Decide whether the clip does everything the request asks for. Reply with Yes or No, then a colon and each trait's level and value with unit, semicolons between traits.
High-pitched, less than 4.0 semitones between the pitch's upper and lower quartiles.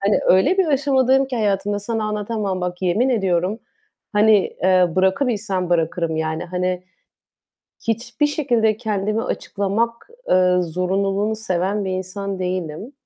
Yes: high, 200 Hz; average, 3.5 semitones